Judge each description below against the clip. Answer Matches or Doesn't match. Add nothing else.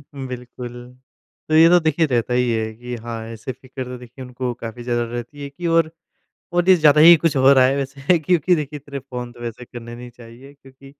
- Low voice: Matches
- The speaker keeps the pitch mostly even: Doesn't match